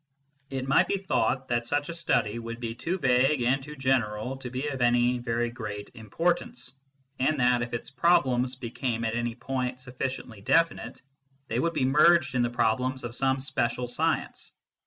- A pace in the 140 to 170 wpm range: No, average, 180 wpm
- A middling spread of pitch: No, narrow, 2.2 semitones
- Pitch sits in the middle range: No, low, 125 Hz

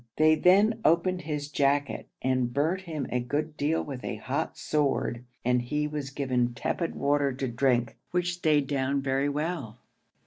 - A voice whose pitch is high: No, medium, 145 Hz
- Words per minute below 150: No, average, 165 wpm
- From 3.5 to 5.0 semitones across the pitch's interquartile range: No, average, 3.1 semitones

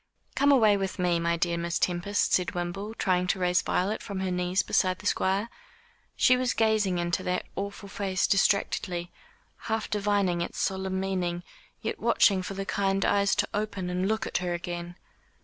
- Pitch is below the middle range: No, high, 190 Hz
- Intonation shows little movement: Yes, narrow, 2.2 semitones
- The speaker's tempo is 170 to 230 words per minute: Yes, average, 180 wpm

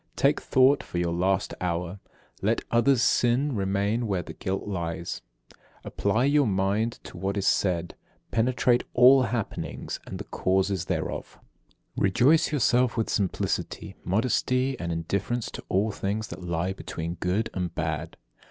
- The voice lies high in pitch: No, low, 100 Hz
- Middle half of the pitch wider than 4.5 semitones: Yes, average, 5.2 semitones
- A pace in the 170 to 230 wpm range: No, average, 150 wpm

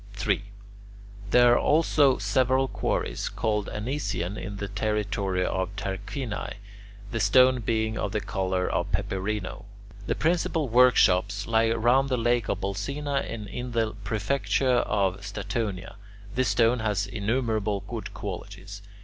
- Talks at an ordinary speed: No, slow, 130 wpm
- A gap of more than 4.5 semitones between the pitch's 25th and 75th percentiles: No, average, 3.7 semitones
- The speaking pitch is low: Yes, low, 110 Hz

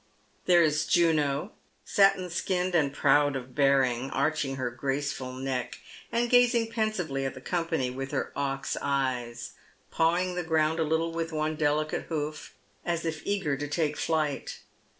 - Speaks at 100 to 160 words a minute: Yes, average, 150 wpm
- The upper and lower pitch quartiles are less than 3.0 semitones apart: No, average, 3.8 semitones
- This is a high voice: No, medium, 155 Hz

